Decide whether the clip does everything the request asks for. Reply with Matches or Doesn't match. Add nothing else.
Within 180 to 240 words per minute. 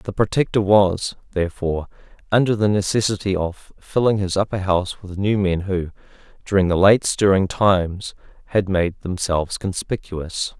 Doesn't match